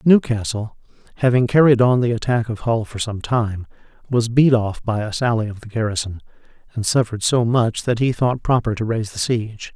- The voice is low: Yes, low, 115 Hz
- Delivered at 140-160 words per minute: No, average, 195 wpm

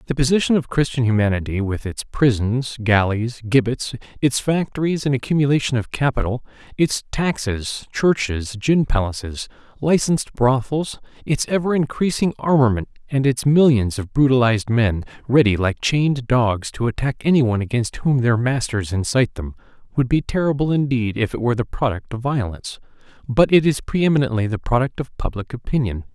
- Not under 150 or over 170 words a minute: Yes, average, 155 wpm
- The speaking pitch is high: No, low, 125 Hz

